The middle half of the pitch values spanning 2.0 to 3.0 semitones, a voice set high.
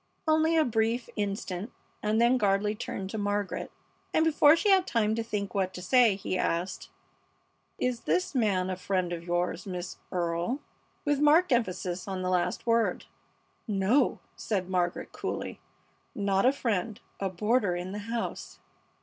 No: average, 4.4 semitones; high, 205 Hz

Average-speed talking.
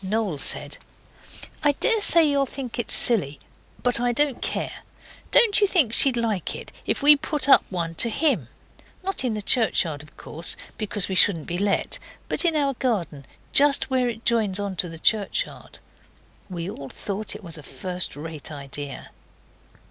Yes: average, 175 wpm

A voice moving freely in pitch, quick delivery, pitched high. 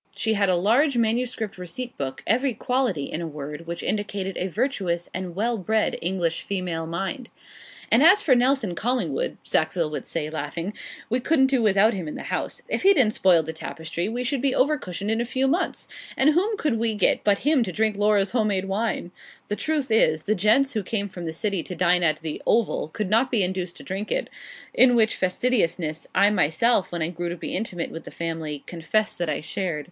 Yes: wide, 5.8 semitones; fast, 215 wpm; high, 200 Hz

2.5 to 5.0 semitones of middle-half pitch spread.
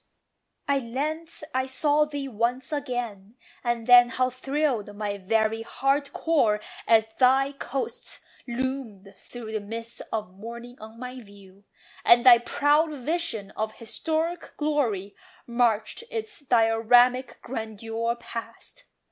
Yes: average, 3.8 semitones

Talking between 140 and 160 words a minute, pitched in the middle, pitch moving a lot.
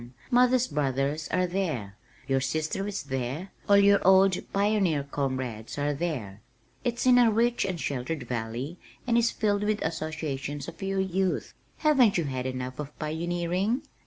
Yes: average, 155 wpm; medium, 165 Hz; wide, 6.7 semitones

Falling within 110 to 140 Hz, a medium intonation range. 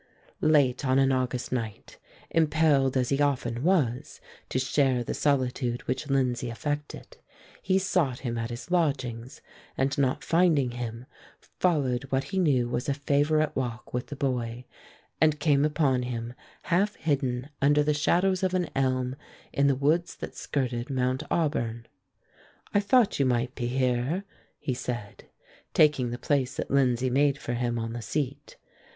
Yes: low, 135 Hz; average, 3.1 semitones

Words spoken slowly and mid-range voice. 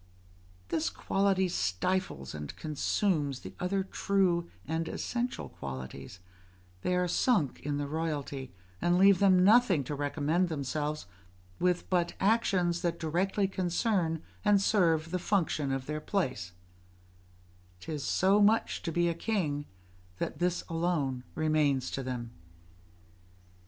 Yes: slow, 125 wpm; medium, 165 Hz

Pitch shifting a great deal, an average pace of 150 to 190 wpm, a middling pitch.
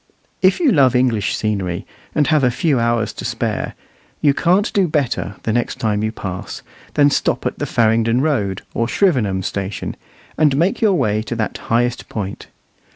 No: wide, 5.7 semitones; average, 175 wpm; low, 120 Hz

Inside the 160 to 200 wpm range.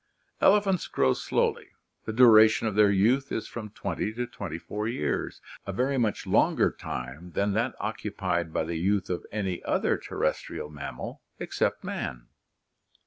No: average, 150 wpm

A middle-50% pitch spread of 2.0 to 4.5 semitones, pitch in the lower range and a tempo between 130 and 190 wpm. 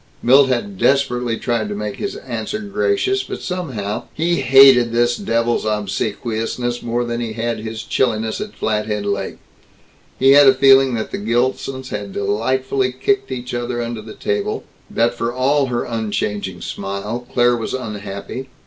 Yes: average, 3.4 semitones; low, 120 Hz; average, 160 wpm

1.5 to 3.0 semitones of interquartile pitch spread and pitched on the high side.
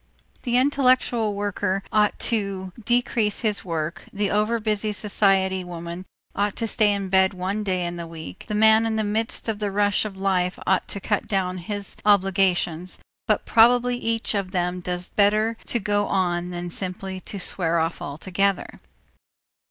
Yes: average, 2.7 semitones; high, 200 Hz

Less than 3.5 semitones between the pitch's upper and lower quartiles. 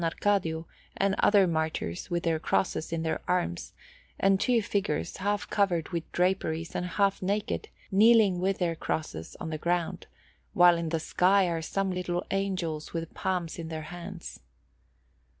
Yes: average, 3.0 semitones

